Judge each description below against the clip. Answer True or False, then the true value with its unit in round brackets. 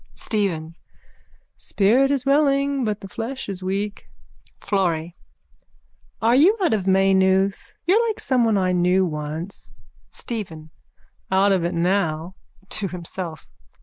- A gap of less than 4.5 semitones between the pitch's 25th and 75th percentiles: False (4.8 semitones)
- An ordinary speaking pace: False (120 wpm)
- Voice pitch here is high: True (195 Hz)